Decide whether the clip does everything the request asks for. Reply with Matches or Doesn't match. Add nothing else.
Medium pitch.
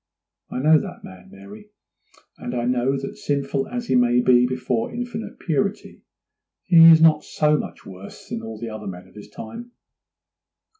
Doesn't match